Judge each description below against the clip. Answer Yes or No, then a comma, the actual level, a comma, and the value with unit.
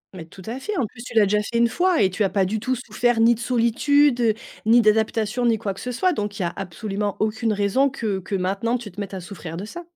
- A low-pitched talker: No, high, 220 Hz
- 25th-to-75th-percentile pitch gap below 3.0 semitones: No, average, 3.3 semitones